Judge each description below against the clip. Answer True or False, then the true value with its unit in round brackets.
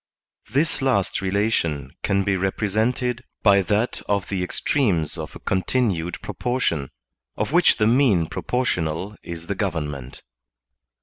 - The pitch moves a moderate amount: False (6.0 semitones)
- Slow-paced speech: True (130 wpm)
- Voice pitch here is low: True (100 Hz)